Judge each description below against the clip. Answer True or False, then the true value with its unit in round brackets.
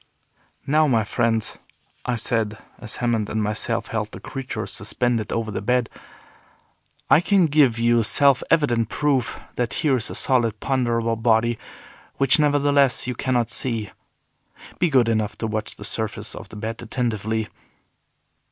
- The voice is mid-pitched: False (115 Hz)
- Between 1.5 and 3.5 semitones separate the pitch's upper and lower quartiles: True (3.0 semitones)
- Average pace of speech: True (150 wpm)